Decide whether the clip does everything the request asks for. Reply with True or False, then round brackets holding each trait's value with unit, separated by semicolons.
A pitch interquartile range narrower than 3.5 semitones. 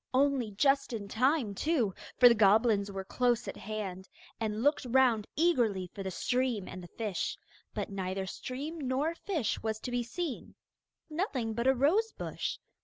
False (5.0 semitones)